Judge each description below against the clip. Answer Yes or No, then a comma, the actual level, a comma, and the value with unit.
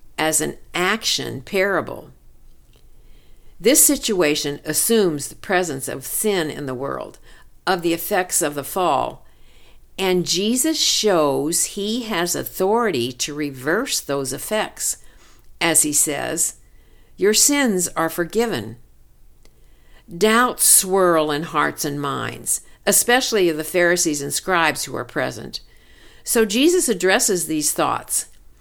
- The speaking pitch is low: No, medium, 175 Hz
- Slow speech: Yes, slow, 120 wpm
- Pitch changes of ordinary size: No, wide, 6.3 semitones